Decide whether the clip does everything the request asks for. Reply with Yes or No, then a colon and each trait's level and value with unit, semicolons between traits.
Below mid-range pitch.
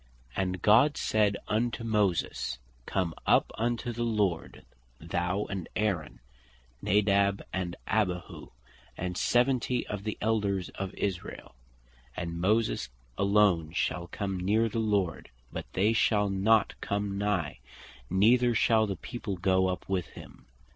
Yes: low, 100 Hz